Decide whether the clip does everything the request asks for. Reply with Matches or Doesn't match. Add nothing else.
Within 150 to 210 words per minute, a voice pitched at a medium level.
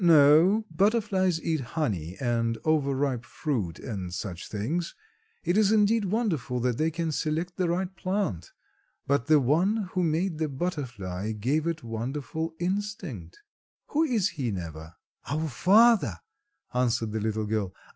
Doesn't match